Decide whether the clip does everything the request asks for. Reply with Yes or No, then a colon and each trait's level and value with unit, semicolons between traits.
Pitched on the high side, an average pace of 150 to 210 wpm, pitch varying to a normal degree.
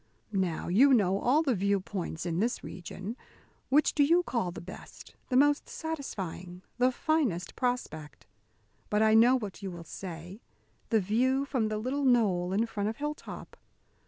No: high, 220 Hz; average, 165 wpm; wide, 6.0 semitones